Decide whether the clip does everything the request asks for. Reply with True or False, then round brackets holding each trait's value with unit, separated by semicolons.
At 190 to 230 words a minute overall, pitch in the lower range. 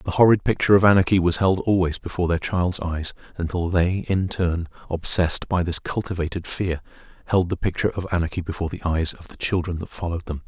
True (200 wpm; 90 Hz)